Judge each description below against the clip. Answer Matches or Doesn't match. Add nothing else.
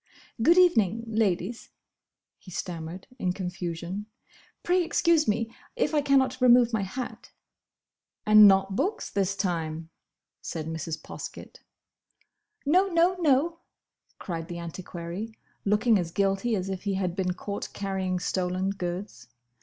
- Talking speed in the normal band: Doesn't match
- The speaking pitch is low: Doesn't match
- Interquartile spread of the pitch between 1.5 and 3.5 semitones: Doesn't match